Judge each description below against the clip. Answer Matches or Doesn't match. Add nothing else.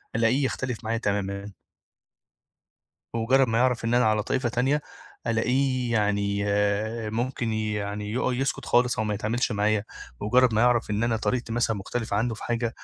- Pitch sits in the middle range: Doesn't match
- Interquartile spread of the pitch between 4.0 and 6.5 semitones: Doesn't match